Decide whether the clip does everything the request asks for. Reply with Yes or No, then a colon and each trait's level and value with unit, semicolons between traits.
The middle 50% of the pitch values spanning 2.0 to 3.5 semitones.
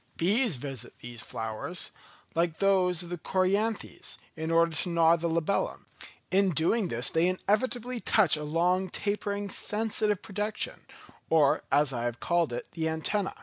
No: average, 4.1 semitones